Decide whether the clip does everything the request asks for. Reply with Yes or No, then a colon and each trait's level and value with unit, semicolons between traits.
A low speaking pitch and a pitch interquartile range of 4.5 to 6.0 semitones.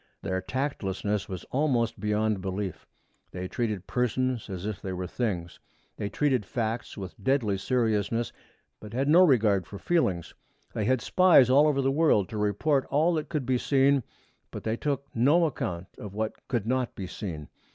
Yes: low, 115 Hz; wide, 5.4 semitones